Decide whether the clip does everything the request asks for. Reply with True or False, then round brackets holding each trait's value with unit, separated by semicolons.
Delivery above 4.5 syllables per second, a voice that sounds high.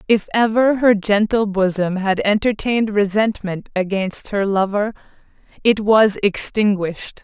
False (4.3 syllables/s; 205 Hz)